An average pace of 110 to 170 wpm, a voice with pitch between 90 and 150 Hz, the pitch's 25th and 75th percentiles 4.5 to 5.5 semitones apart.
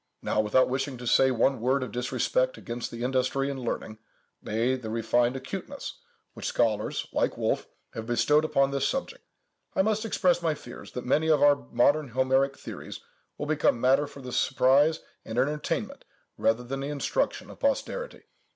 No: average, 165 wpm; low, 135 Hz; average, 3.5 semitones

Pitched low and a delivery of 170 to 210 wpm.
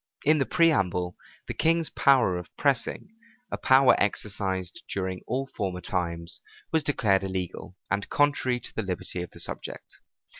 No: low, 100 Hz; average, 150 wpm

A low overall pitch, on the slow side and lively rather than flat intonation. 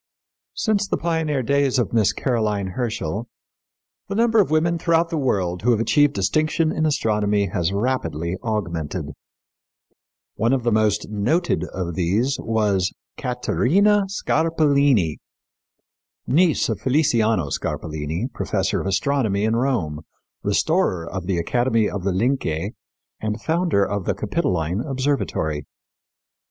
Yes: low, 115 Hz; slow, 125 wpm; wide, 7.2 semitones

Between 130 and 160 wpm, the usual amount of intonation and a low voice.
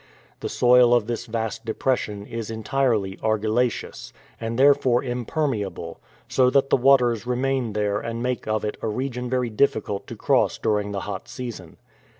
Yes: average, 155 wpm; average, 3.0 semitones; low, 115 Hz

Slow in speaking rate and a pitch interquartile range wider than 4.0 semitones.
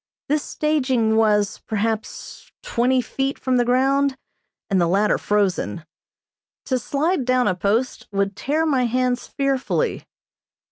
Yes: slow, 130 wpm; average, 4.4 semitones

